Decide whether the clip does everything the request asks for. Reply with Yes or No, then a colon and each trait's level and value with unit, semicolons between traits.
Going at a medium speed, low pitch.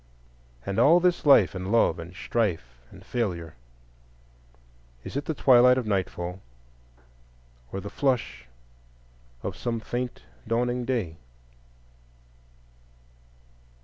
No: slow, 100 wpm; very low, 95 Hz